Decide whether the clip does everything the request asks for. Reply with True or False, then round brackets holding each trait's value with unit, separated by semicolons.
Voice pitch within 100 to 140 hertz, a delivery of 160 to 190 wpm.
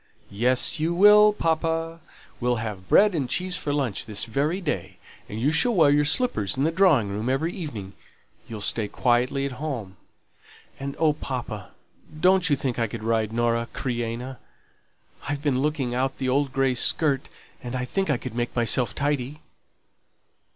True (135 Hz; 170 wpm)